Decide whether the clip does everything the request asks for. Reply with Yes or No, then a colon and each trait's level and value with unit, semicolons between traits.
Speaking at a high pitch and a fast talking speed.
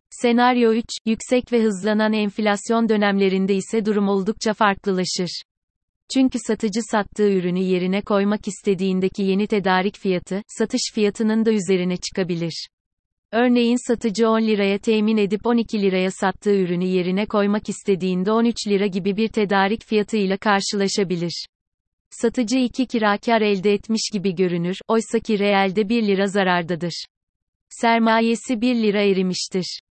No: high, 205 Hz; average, 125 wpm